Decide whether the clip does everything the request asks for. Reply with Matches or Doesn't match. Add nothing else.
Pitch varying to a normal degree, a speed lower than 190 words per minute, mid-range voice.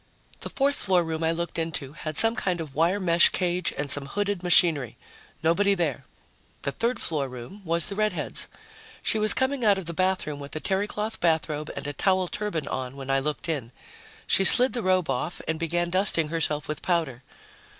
Doesn't match